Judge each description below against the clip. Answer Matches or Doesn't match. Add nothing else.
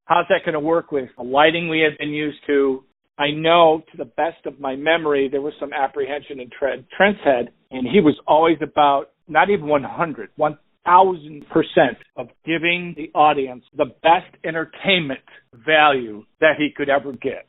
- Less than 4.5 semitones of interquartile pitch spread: Matches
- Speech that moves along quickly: Doesn't match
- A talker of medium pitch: Matches